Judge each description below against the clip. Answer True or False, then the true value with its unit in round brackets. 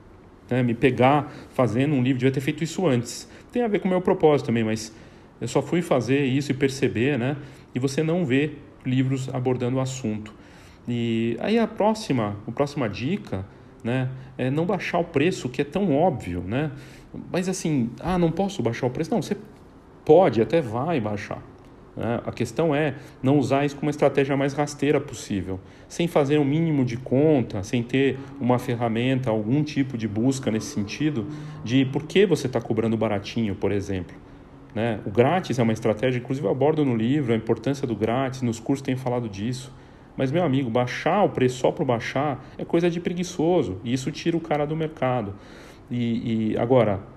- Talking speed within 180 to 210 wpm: True (185 wpm)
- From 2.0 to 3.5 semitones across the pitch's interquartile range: False (4.2 semitones)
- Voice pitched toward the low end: True (130 Hz)